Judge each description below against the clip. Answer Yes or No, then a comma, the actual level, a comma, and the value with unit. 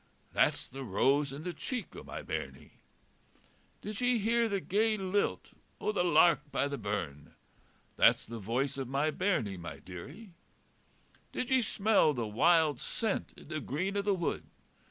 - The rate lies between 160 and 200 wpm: Yes, average, 165 wpm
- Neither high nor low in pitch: Yes, medium, 160 Hz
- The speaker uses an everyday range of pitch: No, wide, 7.8 semitones